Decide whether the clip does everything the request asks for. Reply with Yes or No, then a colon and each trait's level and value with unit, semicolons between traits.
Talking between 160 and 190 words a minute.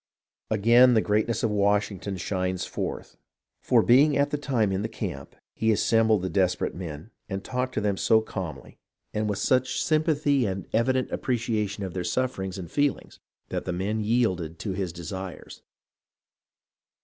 Yes: average, 175 wpm